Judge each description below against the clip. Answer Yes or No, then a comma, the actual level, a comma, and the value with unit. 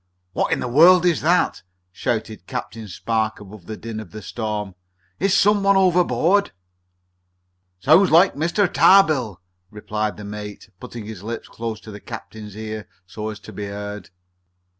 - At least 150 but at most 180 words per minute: Yes, average, 160 wpm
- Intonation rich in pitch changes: Yes, wide, 7.9 semitones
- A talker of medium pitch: No, low, 110 Hz